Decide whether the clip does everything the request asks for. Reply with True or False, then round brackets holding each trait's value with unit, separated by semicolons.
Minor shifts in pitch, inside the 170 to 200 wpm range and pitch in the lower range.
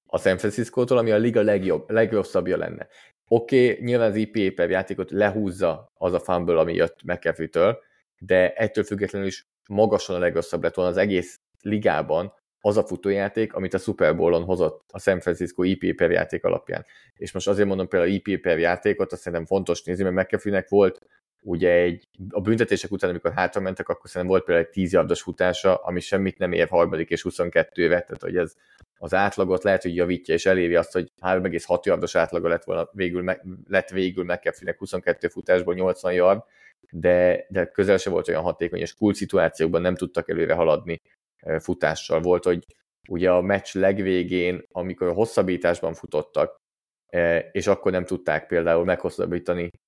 True (2.0 semitones; 175 wpm; 95 Hz)